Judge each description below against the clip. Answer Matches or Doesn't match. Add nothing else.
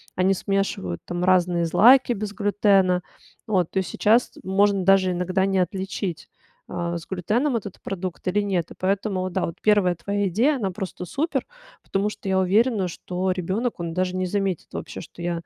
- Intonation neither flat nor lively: Doesn't match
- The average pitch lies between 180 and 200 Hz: Matches